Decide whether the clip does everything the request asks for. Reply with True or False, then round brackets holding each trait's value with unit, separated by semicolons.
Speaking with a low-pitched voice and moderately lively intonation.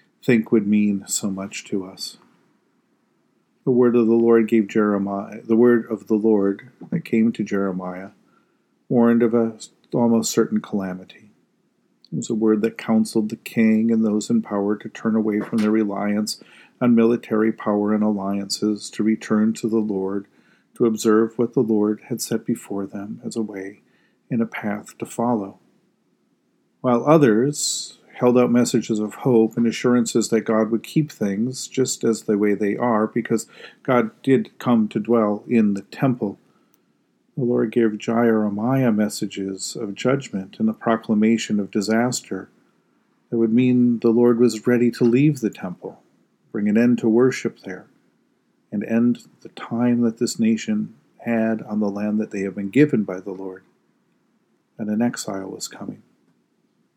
False (110 Hz; 2.3 semitones)